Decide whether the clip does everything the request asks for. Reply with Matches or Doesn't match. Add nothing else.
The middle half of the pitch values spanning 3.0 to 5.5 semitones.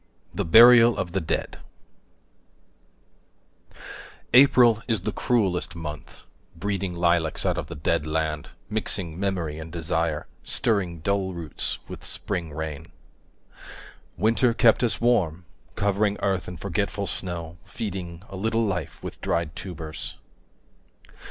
Matches